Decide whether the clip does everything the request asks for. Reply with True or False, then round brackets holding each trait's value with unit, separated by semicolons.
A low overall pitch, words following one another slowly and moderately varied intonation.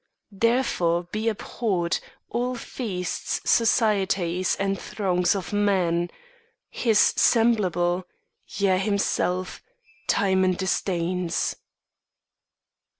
False (190 Hz; 75 wpm; 3.0 semitones)